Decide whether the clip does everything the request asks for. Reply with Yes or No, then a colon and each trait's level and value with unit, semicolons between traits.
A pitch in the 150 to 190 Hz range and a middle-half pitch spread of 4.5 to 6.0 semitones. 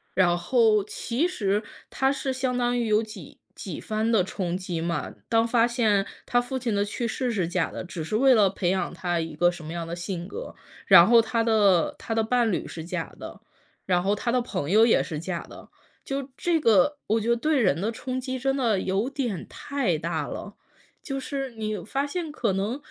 No: high, 220 Hz; average, 5.2 semitones